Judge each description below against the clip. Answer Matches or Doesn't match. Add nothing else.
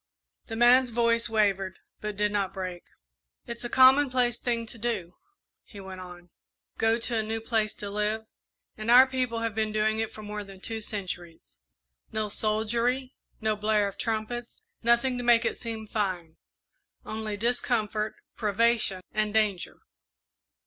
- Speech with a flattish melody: Matches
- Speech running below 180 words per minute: Matches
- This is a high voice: Matches